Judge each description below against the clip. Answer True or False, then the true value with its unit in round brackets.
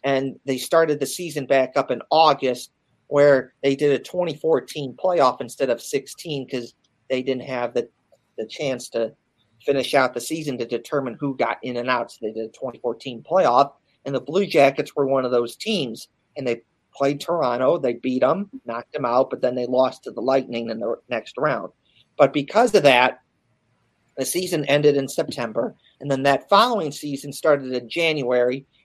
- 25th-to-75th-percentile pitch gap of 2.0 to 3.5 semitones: True (2.9 semitones)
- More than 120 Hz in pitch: True (135 Hz)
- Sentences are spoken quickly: False (185 wpm)